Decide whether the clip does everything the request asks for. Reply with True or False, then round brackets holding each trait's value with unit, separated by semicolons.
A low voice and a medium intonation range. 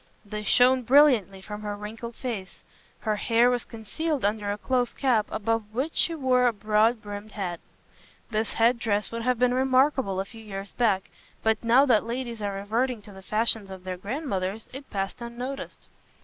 False (225 Hz; 3.4 semitones)